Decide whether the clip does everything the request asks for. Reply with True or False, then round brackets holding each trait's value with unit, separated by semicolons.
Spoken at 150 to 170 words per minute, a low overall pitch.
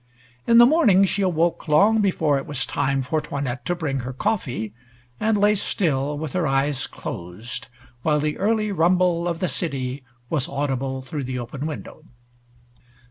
False (165 wpm; 150 Hz)